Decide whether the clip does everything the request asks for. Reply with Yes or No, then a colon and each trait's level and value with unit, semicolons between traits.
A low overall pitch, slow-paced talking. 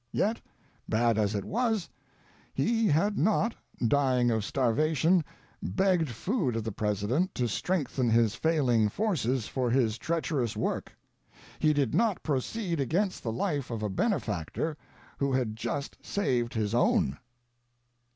No: low, 130 Hz; average, 145 wpm